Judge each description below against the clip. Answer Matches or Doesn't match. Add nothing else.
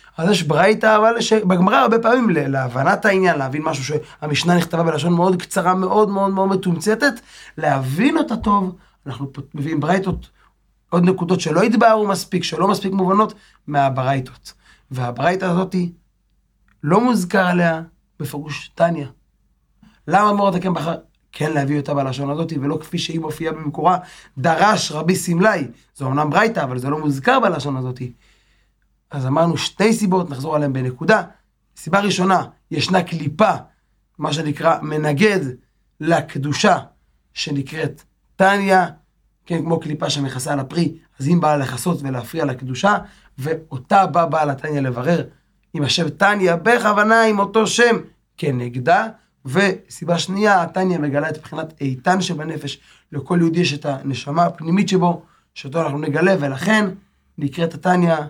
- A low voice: Doesn't match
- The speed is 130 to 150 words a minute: Matches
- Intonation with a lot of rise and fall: Doesn't match